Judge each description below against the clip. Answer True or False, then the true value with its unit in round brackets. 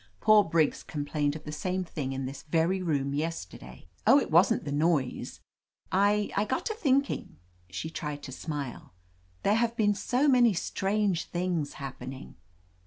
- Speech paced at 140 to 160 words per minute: False (170 wpm)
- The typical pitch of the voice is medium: True (165 Hz)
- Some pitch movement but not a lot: False (6.2 semitones)